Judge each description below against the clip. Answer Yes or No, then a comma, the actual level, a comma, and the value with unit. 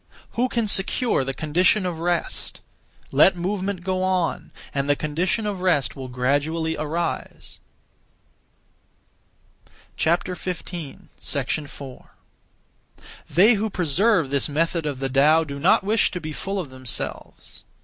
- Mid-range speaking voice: Yes, medium, 165 Hz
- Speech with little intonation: No, average, 4.6 semitones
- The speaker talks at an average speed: No, slow, 120 wpm